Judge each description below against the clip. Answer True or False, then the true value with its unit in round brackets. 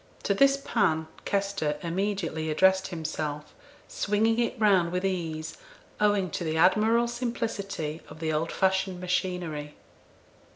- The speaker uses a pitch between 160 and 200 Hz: True (185 Hz)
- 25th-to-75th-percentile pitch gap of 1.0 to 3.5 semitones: False (4.3 semitones)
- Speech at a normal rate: False (125 wpm)